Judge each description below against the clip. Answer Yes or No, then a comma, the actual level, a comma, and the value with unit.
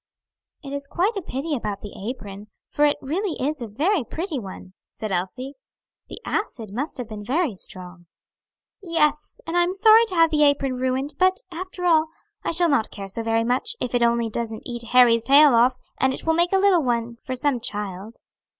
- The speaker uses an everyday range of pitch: No, wide, 6.3 semitones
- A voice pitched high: Yes, very high, 265 Hz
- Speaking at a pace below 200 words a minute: No, fast, 205 wpm